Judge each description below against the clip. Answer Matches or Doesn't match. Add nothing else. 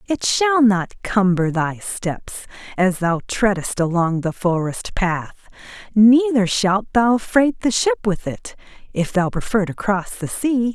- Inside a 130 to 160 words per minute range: Matches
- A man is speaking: Doesn't match